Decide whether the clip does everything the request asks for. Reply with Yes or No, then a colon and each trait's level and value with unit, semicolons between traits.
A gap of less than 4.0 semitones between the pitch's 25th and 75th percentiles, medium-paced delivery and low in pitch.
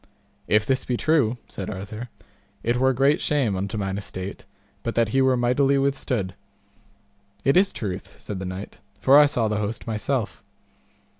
No: average, 4.7 semitones; average, 165 wpm; low, 115 Hz